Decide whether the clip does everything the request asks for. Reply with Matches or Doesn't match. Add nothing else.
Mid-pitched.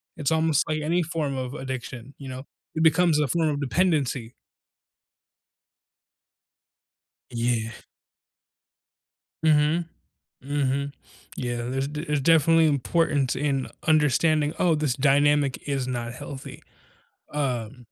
Matches